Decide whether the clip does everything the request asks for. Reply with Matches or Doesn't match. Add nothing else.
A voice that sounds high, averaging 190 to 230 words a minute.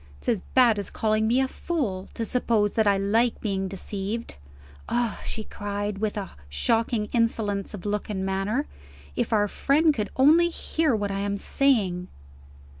Doesn't match